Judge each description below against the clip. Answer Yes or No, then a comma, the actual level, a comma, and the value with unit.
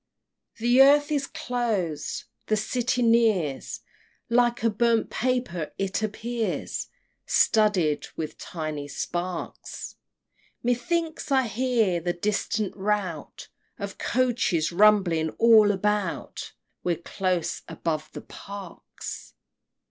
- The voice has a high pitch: Yes, high, 210 Hz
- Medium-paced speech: No, slow, 100 wpm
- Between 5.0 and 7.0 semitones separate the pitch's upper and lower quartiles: Yes, wide, 5.5 semitones